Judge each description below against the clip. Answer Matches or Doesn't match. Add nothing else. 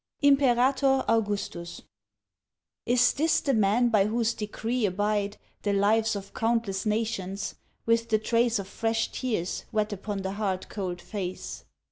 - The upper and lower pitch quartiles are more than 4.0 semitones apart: Doesn't match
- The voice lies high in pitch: Matches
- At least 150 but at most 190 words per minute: Doesn't match